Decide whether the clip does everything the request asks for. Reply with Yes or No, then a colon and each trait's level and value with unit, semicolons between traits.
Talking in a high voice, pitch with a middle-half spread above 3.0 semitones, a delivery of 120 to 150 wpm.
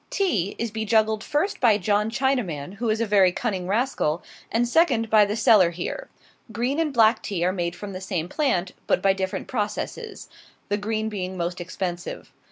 No: high, 210 Hz; average, 4.0 semitones; average, 180 wpm